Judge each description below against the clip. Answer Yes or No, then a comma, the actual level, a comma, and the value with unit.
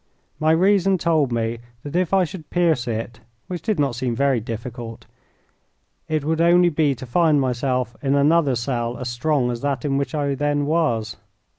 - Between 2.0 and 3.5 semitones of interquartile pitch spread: No, average, 5.0 semitones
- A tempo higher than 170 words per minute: Yes, average, 180 wpm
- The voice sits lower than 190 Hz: Yes, medium, 140 Hz